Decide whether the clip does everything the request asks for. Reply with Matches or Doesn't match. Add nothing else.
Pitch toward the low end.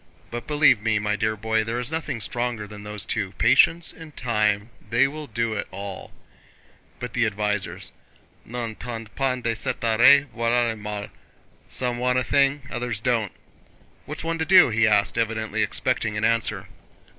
Matches